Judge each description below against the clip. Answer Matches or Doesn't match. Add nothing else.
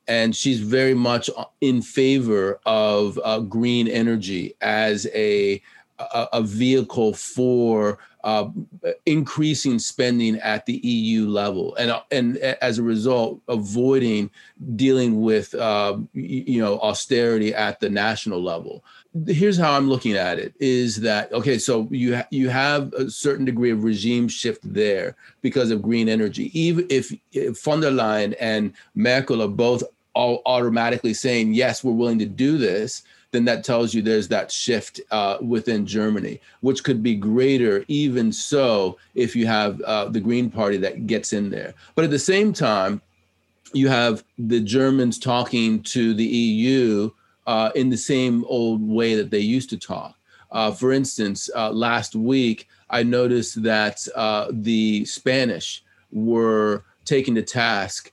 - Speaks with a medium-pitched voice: Doesn't match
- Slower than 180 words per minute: Matches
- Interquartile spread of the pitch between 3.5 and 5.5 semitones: Doesn't match